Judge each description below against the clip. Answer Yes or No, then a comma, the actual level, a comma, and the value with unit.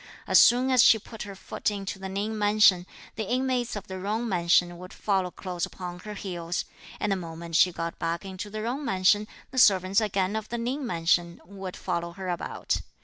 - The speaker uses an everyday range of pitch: Yes, average, 3.3 semitones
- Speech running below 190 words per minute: No, fast, 205 wpm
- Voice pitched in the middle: No, high, 195 Hz